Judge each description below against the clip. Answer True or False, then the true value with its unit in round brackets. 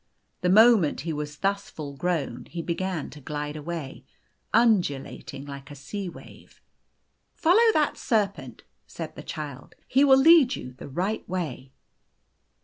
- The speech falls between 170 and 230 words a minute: False (145 wpm)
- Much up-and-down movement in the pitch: True (6.8 semitones)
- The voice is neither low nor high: True (175 Hz)